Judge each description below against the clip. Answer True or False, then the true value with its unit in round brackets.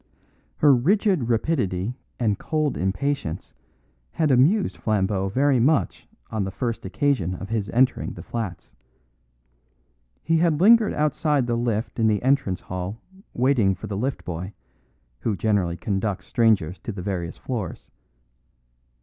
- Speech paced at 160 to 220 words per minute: False (135 wpm)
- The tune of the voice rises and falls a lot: True (6.4 semitones)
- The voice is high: False (115 Hz)